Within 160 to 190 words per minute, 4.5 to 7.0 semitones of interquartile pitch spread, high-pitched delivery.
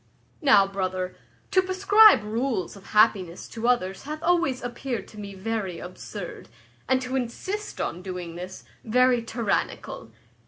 No: slow, 135 wpm; wide, 5.6 semitones; high, 225 Hz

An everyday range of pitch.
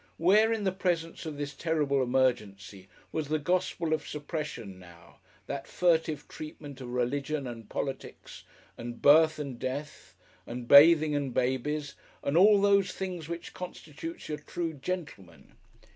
Yes: average, 4.3 semitones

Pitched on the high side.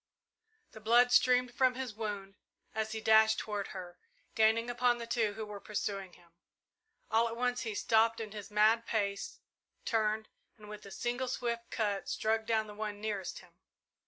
Yes: high, 220 Hz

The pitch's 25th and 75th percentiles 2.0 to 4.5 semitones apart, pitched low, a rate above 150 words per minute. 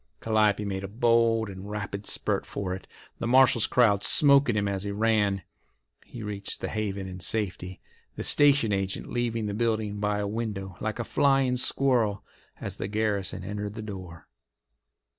Yes: narrow, 2.6 semitones; low, 105 Hz; average, 165 wpm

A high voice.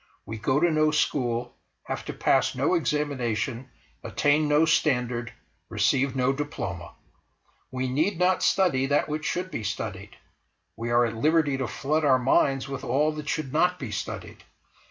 No: low, 135 Hz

